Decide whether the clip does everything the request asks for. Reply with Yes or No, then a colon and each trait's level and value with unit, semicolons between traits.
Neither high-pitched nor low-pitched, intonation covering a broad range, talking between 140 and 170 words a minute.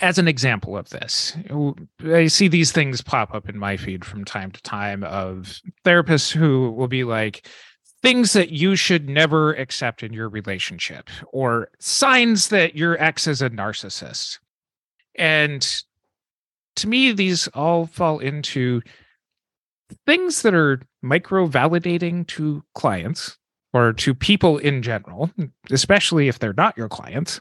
Yes: medium, 150 Hz; wide, 6.8 semitones; average, 145 wpm